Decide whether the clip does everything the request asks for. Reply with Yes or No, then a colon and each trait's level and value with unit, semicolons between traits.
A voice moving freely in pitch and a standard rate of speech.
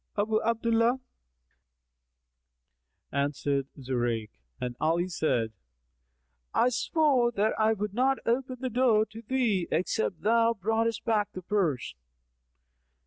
No: wide, 6.1 semitones; slow, 110 wpm